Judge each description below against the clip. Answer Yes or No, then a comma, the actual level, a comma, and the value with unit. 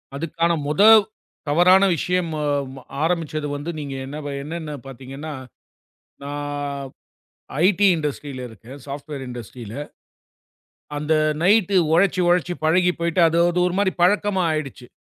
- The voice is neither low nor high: Yes, medium, 155 Hz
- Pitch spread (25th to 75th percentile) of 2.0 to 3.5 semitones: No, average, 3.9 semitones